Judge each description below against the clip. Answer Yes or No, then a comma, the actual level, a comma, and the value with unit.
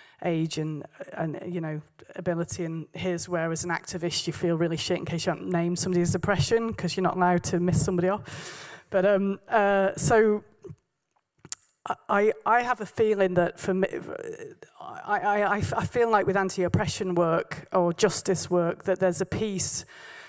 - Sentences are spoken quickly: No, average, 175 wpm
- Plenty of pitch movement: No, average, 3.0 semitones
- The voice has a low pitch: No, medium, 180 Hz